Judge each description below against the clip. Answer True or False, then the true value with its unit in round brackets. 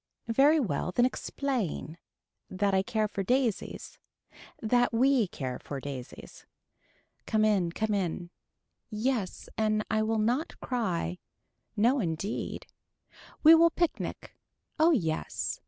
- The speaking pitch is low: False (215 Hz)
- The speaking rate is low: True (120 wpm)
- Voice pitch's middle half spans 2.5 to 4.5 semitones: False (5.5 semitones)